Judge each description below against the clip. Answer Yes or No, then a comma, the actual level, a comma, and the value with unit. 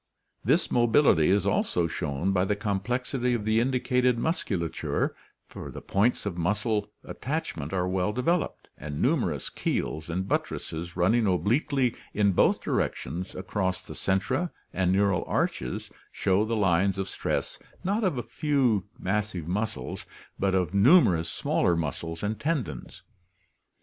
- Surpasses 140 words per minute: No, slow, 135 wpm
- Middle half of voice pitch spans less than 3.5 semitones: No, average, 5.1 semitones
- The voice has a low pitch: Yes, low, 100 Hz